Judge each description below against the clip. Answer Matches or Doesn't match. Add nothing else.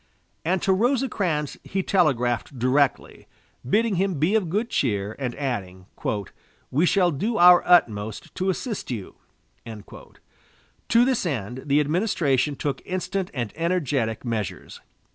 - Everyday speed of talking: Doesn't match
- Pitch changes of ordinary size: Doesn't match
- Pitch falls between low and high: Matches